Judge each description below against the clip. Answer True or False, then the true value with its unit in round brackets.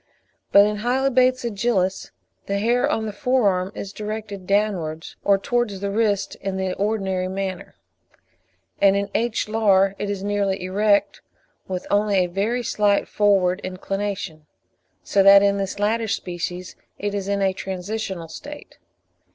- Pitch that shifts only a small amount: True (1.9 semitones)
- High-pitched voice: True (200 Hz)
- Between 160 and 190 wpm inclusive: False (150 wpm)